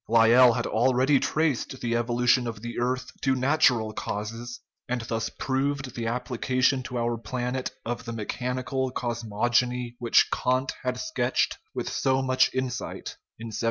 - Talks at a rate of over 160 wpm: No, average, 155 wpm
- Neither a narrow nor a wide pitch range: No, narrow, 1.7 semitones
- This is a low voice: Yes, low, 125 Hz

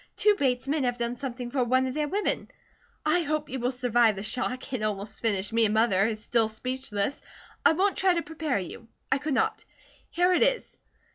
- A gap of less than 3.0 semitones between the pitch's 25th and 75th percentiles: No, average, 5.1 semitones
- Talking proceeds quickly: Yes, fast, 210 wpm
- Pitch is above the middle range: Yes, very high, 255 Hz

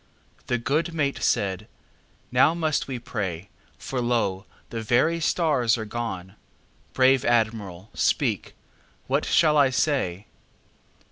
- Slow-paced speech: Yes, slow, 110 wpm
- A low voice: Yes, low, 120 Hz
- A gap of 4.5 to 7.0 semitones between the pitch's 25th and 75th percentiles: Yes, wide, 5.4 semitones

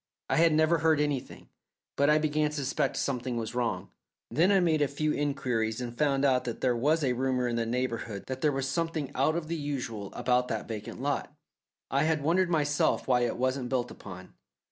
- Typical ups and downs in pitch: Yes, average, 3.7 semitones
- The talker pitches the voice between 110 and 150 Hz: Yes, low, 135 Hz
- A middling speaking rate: No, fast, 210 wpm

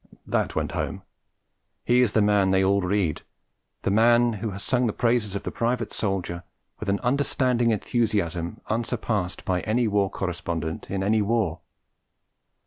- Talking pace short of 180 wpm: Yes, average, 155 wpm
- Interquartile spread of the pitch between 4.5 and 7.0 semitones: No, average, 3.5 semitones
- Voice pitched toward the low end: Yes, low, 105 Hz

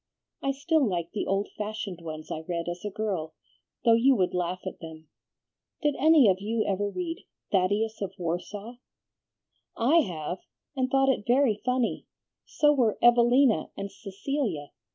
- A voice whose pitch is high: Yes, high, 210 Hz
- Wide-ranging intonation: Yes, wide, 6.1 semitones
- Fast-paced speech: No, average, 155 wpm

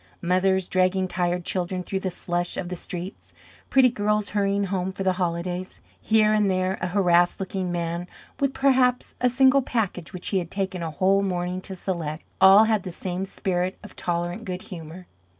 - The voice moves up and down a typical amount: No, narrow, 2.1 semitones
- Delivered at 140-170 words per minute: No, average, 185 wpm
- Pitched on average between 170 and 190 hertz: Yes, medium, 185 Hz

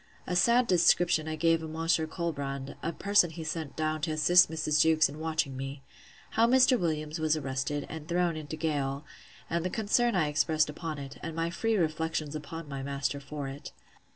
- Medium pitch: Yes, medium, 155 Hz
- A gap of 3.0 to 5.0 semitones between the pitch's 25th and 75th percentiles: No, narrow, 2.5 semitones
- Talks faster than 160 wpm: Yes, average, 190 wpm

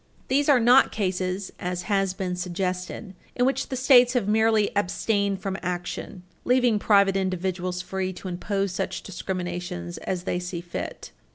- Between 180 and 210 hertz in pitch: Yes, high, 190 Hz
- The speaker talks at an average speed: Yes, average, 155 wpm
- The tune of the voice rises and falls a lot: No, average, 3.1 semitones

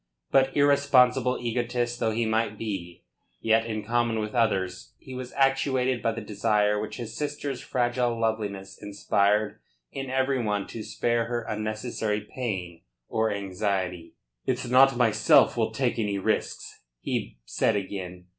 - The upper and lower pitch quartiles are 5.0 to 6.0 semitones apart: No, average, 3.2 semitones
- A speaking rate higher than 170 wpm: No, average, 145 wpm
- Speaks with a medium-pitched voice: No, low, 110 Hz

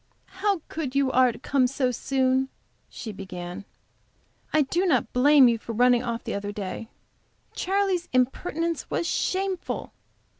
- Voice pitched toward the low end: No, very high, 260 Hz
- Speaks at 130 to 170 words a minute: Yes, average, 145 wpm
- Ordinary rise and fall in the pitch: No, wide, 5.9 semitones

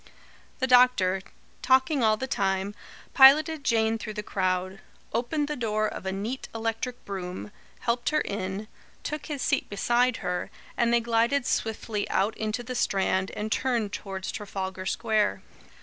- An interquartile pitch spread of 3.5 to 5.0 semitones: Yes, average, 4.2 semitones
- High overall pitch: Yes, high, 220 Hz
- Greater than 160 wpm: No, average, 150 wpm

